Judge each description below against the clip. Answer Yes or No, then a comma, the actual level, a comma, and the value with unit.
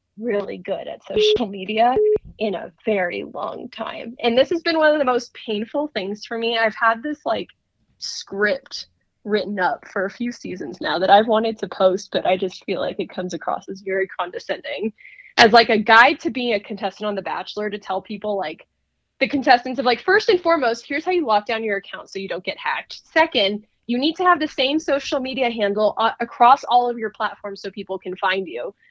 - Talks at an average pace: No, fast, 220 wpm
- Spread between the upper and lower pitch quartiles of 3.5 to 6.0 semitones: Yes, average, 4.6 semitones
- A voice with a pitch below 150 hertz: No, high, 220 Hz